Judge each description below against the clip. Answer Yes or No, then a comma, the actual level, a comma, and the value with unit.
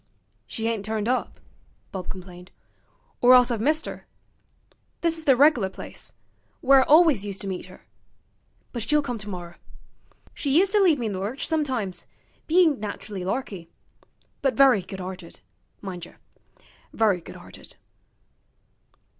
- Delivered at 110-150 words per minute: Yes, average, 145 wpm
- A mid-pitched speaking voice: No, high, 225 Hz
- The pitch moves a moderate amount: No, wide, 6.5 semitones